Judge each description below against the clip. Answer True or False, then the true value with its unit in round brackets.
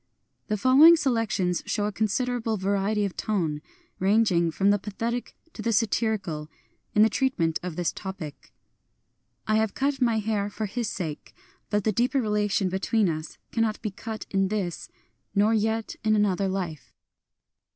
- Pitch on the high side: True (210 Hz)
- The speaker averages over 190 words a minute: False (170 wpm)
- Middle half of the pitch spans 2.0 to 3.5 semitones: True (2.8 semitones)